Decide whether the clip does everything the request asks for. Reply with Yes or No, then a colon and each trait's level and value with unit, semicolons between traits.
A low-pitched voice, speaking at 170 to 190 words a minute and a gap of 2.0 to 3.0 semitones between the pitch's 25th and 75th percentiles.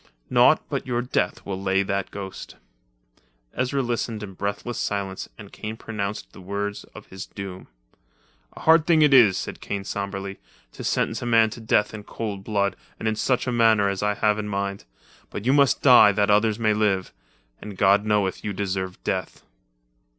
Yes: low, 105 Hz; average, 180 wpm; narrow, 2.4 semitones